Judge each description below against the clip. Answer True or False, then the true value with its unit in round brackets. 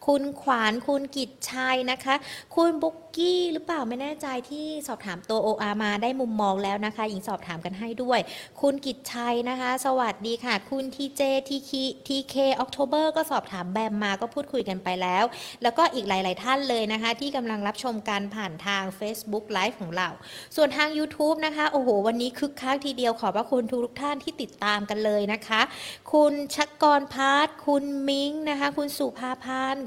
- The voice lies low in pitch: False (255 Hz)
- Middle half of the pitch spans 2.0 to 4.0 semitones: False (4.7 semitones)